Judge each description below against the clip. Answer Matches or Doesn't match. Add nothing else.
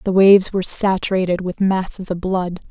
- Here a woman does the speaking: Matches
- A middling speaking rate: Matches